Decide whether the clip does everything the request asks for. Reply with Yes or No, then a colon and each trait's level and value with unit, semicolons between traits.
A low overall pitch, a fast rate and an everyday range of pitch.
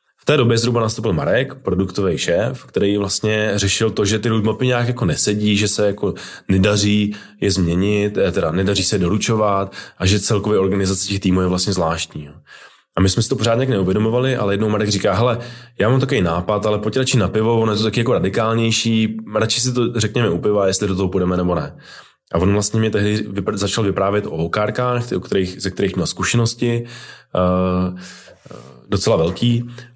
Yes: low, 105 Hz; fast, 185 wpm; average, 3.2 semitones